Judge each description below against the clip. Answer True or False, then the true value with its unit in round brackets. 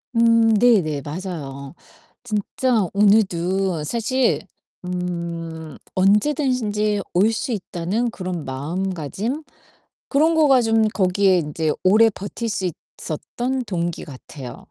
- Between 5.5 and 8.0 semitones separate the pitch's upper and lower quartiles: False (5.1 semitones)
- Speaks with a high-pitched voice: True (195 Hz)